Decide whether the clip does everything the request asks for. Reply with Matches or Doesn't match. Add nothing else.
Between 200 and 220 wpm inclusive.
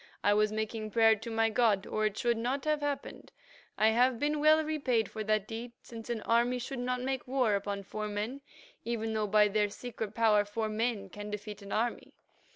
Matches